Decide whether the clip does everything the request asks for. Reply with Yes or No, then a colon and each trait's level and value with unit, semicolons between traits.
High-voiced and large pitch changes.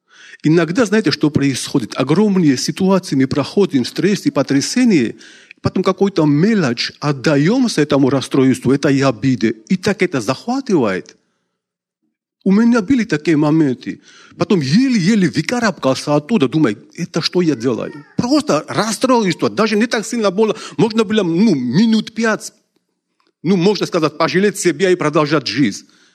No: medium, 175 Hz; wide, 6.7 semitones